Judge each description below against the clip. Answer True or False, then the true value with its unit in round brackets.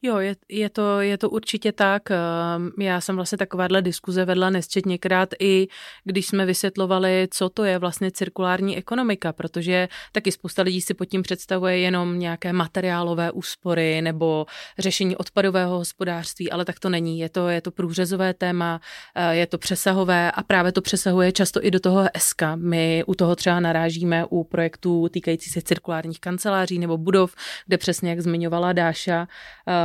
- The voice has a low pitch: False (180 Hz)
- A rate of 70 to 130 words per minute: False (165 wpm)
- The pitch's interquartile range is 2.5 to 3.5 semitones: False (1.9 semitones)